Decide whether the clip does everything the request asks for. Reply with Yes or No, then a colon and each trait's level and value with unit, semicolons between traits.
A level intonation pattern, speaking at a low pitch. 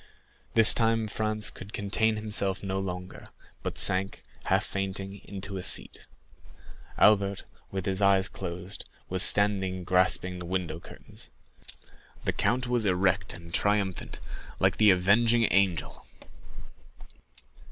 Yes: narrow, 2.3 semitones; very low, 95 Hz